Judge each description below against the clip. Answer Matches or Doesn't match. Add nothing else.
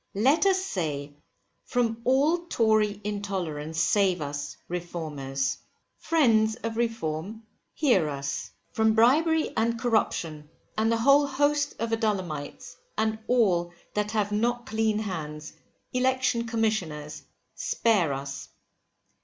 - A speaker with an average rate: Doesn't match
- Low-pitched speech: Doesn't match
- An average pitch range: Doesn't match